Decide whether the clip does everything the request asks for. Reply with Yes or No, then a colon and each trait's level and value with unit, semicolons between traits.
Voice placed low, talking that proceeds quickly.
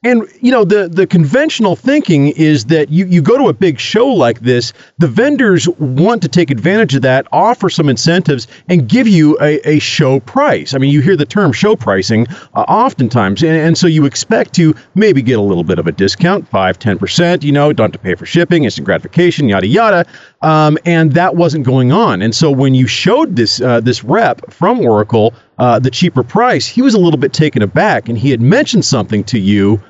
No: medium, 155 Hz; fast, 220 wpm